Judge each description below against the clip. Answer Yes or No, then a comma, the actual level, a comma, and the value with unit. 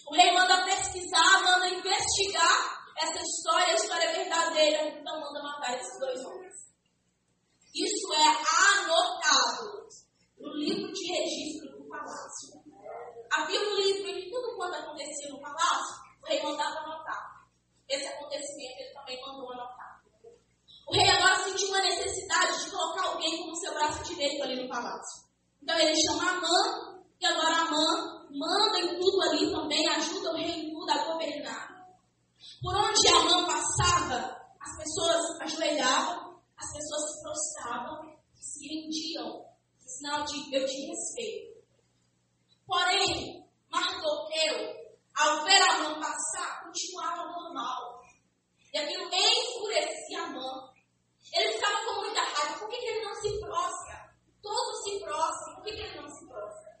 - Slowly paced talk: No, average, 145 wpm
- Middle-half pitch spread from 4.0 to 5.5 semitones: No, average, 3.5 semitones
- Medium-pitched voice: No, very high, 330 Hz